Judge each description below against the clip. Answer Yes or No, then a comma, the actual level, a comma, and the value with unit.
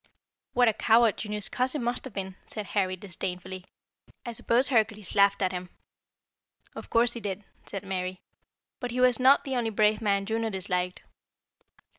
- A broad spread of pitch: No, average, 3.8 semitones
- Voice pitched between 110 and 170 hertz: No, high, 210 Hz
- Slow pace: No, average, 165 wpm